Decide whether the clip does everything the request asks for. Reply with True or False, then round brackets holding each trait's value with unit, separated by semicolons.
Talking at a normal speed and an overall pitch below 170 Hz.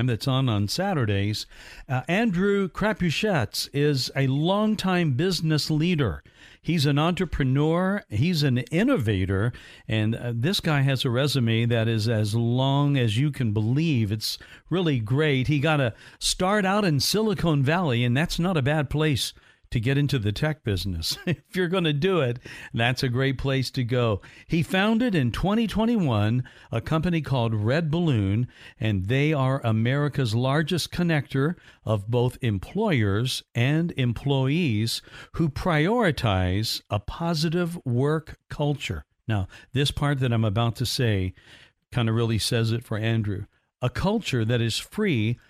True (150 wpm; 135 Hz)